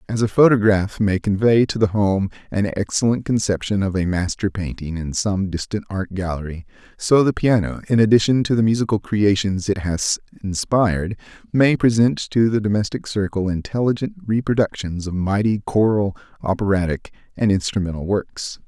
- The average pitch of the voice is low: Yes, low, 105 Hz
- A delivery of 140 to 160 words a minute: Yes, average, 150 wpm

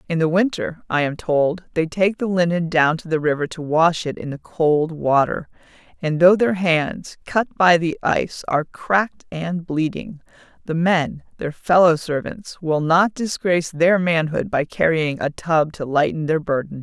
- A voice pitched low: No, medium, 165 Hz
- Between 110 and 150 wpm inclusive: No, average, 180 wpm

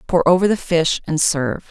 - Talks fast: Yes, fast, 210 wpm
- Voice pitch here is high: No, medium, 165 Hz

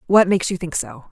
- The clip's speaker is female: Yes, female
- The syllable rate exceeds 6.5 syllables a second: Yes, 6.7 syllables/s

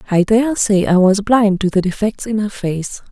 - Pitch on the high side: Yes, high, 205 Hz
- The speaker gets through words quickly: Yes, fast, 210 wpm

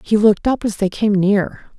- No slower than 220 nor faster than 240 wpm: Yes, fast, 235 wpm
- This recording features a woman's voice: Yes, female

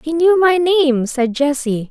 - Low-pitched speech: No, very high, 295 Hz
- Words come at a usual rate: Yes, average, 190 wpm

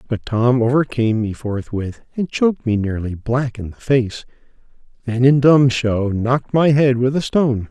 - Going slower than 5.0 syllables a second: Yes, 4.7 syllables/s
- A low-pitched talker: Yes, low, 120 Hz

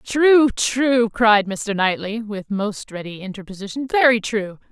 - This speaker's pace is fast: No, average, 140 wpm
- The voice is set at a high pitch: Yes, high, 215 Hz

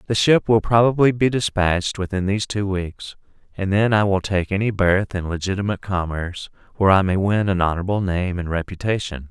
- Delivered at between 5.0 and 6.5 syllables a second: Yes, 5.8 syllables/s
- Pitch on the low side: Yes, low, 100 Hz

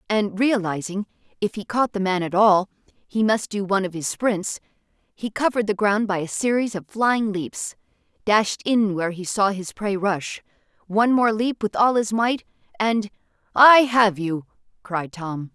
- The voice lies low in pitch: No, high, 205 Hz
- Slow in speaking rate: No, average, 175 wpm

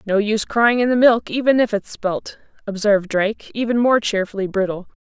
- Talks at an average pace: Yes, average, 190 wpm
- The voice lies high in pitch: Yes, high, 215 Hz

